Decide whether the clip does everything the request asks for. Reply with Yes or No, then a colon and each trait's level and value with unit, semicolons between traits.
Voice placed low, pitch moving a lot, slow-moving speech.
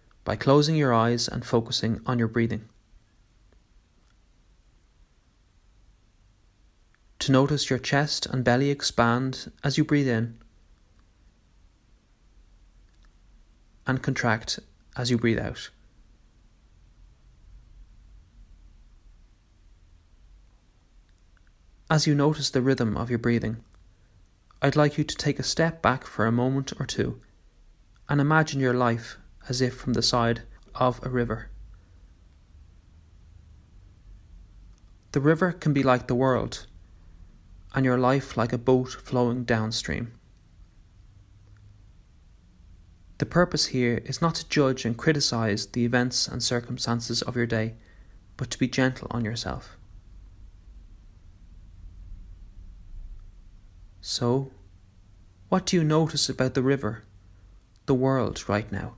Yes: low, 105 Hz; wide, 5.7 semitones; slow, 110 wpm